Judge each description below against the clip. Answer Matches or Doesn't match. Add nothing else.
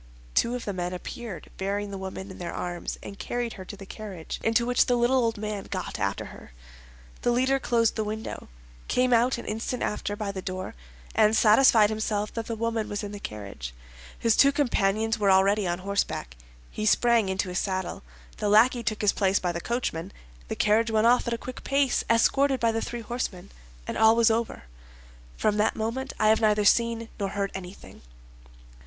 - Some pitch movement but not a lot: Matches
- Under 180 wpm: Doesn't match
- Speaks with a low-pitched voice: Doesn't match